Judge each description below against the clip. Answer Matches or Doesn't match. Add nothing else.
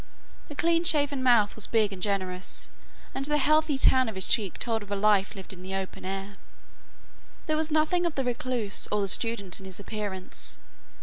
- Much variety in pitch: Matches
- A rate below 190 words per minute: Doesn't match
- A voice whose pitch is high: Matches